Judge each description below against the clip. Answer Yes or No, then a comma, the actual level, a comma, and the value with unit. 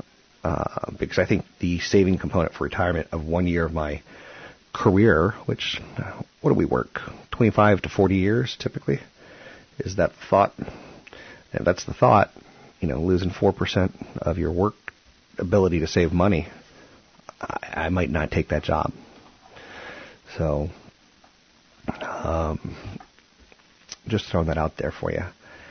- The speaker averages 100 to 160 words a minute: Yes, average, 140 wpm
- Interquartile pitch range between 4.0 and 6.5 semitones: No, average, 3.0 semitones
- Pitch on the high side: No, very low, 90 Hz